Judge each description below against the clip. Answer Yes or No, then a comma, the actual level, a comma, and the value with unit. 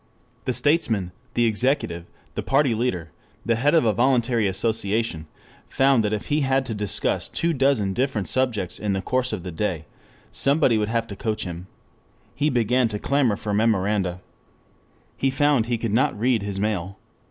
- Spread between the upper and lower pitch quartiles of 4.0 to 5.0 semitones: Yes, average, 4.3 semitones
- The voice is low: Yes, low, 115 Hz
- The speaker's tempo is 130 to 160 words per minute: No, average, 175 wpm